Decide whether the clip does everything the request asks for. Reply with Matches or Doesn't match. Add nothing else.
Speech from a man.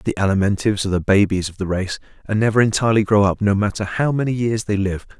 Matches